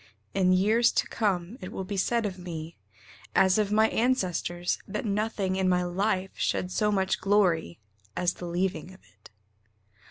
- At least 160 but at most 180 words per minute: Yes, average, 165 wpm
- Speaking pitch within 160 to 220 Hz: Yes, high, 190 Hz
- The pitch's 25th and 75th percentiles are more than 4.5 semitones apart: No, average, 2.7 semitones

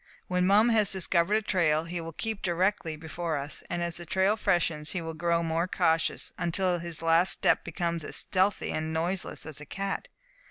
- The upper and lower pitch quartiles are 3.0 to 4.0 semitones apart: No, narrow, 2.6 semitones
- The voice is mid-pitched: Yes, medium, 170 Hz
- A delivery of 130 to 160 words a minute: No, average, 200 wpm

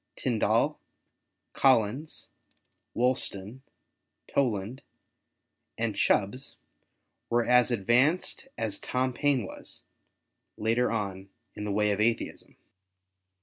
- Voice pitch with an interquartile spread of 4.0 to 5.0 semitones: No, average, 3.6 semitones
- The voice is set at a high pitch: No, low, 115 Hz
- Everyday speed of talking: No, slow, 90 wpm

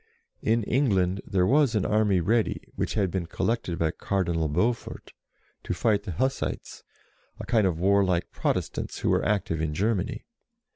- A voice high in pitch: No, low, 100 Hz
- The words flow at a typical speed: Yes, average, 155 wpm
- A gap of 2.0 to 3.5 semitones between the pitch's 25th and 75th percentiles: No, average, 3.9 semitones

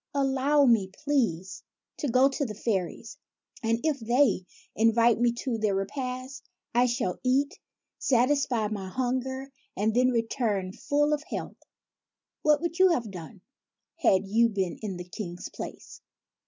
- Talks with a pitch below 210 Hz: No, high, 240 Hz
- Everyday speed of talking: Yes, average, 145 wpm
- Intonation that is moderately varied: Yes, average, 4.7 semitones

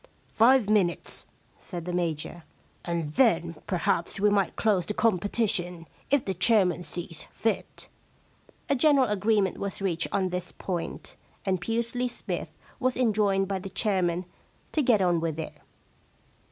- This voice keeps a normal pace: Yes, average, 150 wpm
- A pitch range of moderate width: Yes, average, 4.1 semitones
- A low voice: No, high, 195 Hz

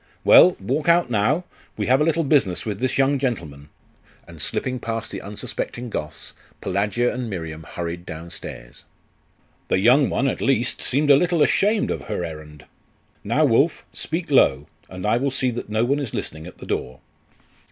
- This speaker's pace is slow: No, average, 175 wpm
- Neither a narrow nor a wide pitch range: No, wide, 7.7 semitones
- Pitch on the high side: No, low, 120 Hz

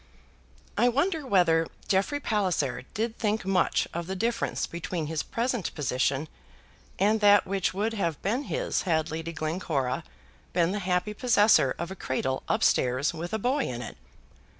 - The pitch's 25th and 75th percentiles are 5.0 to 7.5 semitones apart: Yes, wide, 5.4 semitones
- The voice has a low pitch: No, medium, 185 Hz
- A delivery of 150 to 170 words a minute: Yes, average, 160 wpm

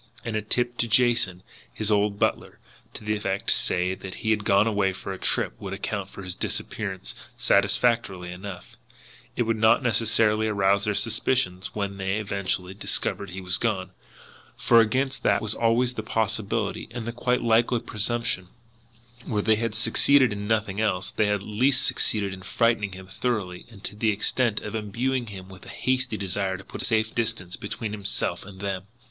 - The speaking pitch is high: No, low, 105 Hz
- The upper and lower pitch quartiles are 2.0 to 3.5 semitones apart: Yes, average, 2.8 semitones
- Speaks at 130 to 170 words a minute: No, average, 185 wpm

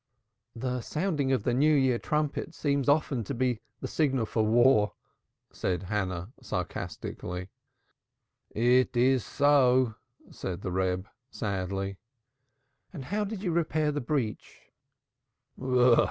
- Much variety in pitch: Yes, wide, 6.4 semitones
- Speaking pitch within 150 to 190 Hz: No, low, 125 Hz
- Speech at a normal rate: No, slow, 120 wpm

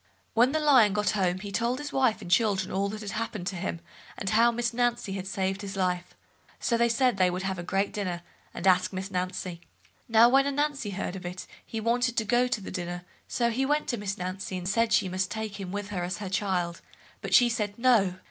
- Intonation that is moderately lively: Yes, average, 4.1 semitones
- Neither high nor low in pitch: No, high, 205 Hz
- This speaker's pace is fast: Yes, fast, 230 wpm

